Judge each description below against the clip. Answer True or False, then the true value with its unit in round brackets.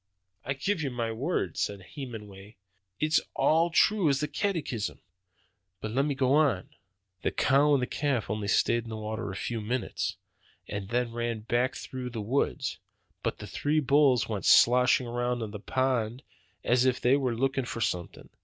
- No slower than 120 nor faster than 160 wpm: False (180 wpm)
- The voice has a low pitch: True (125 Hz)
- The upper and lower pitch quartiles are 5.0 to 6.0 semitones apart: False (3.8 semitones)